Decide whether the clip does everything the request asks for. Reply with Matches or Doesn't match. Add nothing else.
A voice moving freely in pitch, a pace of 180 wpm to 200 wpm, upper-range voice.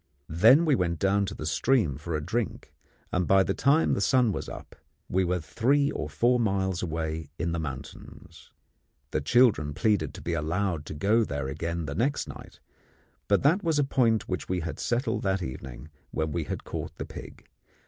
Doesn't match